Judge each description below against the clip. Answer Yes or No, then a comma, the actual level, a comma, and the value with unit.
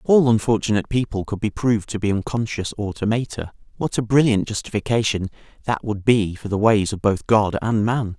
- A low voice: Yes, low, 110 Hz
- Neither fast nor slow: Yes, average, 190 wpm